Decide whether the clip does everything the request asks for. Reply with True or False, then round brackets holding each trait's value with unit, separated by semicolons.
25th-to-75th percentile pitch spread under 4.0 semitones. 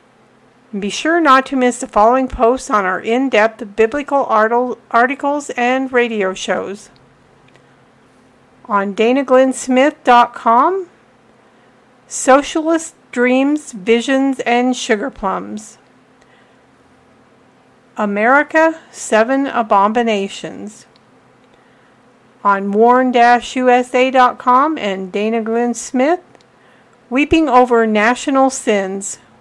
True (3.1 semitones)